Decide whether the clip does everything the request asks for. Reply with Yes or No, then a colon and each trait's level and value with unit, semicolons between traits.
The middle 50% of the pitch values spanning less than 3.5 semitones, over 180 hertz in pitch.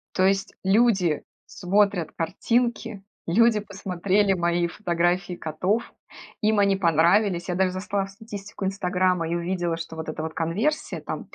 Yes: average, 2.9 semitones; high, 190 Hz